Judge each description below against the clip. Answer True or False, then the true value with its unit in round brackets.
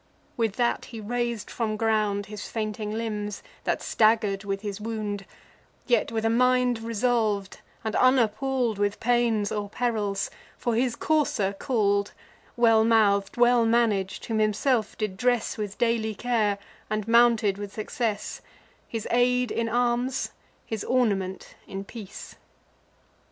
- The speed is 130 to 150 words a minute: True (135 wpm)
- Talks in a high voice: True (220 Hz)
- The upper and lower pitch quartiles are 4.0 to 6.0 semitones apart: False (2.5 semitones)